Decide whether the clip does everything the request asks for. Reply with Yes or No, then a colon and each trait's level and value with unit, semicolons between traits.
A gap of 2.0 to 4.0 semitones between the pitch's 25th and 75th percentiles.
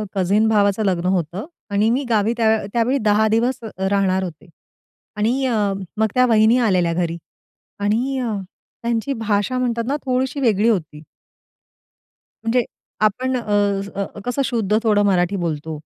Yes: average, 3.5 semitones